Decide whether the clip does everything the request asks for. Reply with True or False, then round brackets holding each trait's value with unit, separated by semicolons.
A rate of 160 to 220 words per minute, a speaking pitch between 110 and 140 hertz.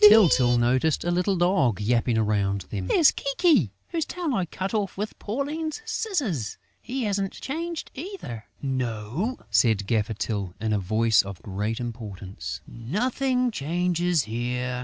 False (140 wpm; 135 Hz)